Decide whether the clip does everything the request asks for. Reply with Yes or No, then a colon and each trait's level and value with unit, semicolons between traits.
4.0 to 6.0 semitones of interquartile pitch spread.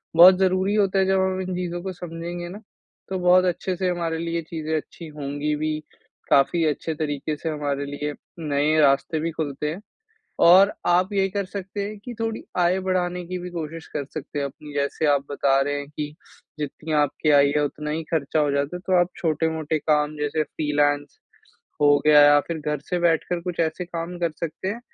No: average, 3.4 semitones